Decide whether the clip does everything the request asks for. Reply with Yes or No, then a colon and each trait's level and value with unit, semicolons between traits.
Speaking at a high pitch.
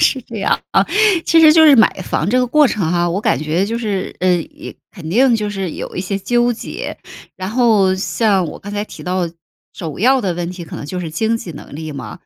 Yes: high, 195 Hz